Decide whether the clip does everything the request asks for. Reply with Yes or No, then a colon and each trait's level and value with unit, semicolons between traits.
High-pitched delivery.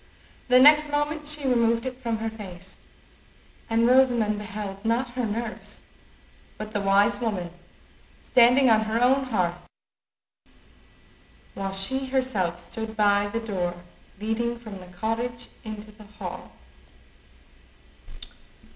Yes: high, 225 Hz